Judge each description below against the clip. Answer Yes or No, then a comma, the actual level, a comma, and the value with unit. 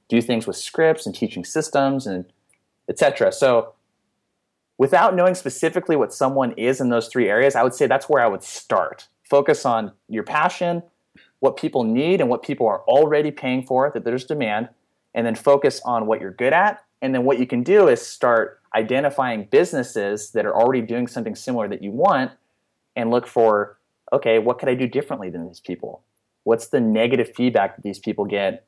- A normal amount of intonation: Yes, average, 3.9 semitones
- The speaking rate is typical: Yes, average, 195 wpm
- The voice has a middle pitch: No, low, 125 Hz